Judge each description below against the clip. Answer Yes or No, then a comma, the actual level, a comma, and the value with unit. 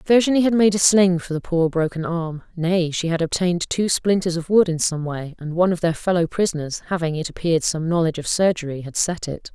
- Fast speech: Yes, fast, 220 wpm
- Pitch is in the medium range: Yes, medium, 170 Hz